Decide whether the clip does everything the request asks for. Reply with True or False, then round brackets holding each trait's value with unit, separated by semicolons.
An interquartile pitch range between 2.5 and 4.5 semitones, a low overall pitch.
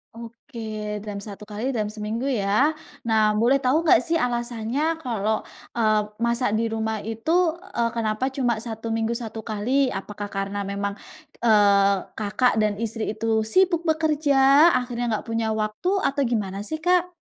False (3.2 semitones; 225 Hz)